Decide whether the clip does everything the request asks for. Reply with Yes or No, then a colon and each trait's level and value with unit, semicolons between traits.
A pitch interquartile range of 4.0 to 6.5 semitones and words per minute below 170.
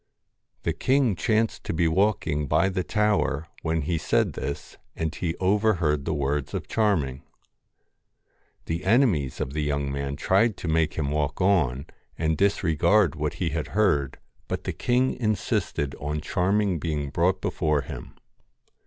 Yes: average, 5.1 semitones; average, 155 wpm